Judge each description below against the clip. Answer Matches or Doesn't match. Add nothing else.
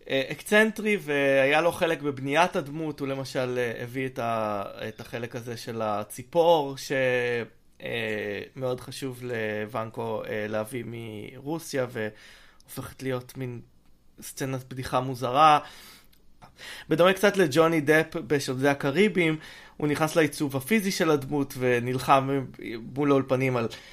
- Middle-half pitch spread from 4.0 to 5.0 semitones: Matches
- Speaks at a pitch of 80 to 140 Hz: Matches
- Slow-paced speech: Doesn't match